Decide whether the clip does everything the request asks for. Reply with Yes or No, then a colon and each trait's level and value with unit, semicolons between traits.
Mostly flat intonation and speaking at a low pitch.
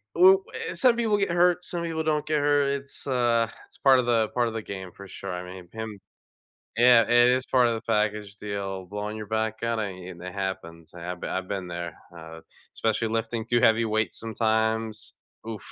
No: average, 4.3 semitones; low, 110 Hz